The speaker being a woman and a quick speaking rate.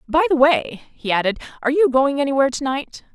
Yes: female; fast, 210 wpm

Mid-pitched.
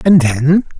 Yes: medium, 155 Hz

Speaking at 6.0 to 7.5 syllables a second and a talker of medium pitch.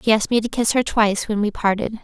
No: 6.7 syllables/s; high, 215 Hz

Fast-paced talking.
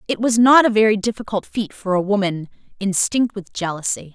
No: average, 190 wpm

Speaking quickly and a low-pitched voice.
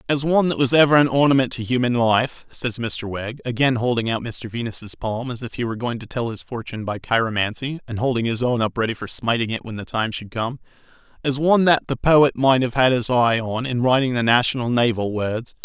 Yes: fast, 235 wpm; low, 120 Hz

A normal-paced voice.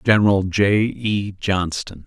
No: slow, 115 wpm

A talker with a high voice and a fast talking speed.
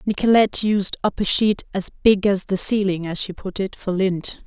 Yes: high, 195 Hz; fast, 215 wpm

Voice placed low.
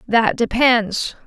No: high, 225 Hz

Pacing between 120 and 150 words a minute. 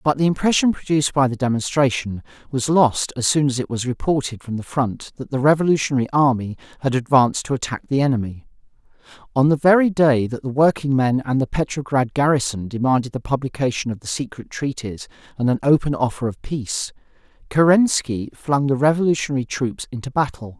No: average, 170 wpm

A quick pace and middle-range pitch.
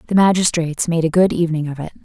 Yes: fast, 235 wpm; medium, 170 Hz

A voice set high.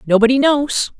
Yes: very high, 250 Hz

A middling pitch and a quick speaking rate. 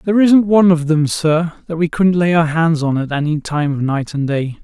Yes: medium, 160 Hz; fast, 260 wpm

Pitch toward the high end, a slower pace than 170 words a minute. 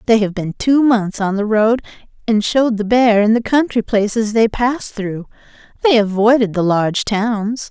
No: high, 220 Hz; average, 185 wpm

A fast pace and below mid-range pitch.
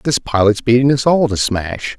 Yes: fast, 210 wpm; low, 120 Hz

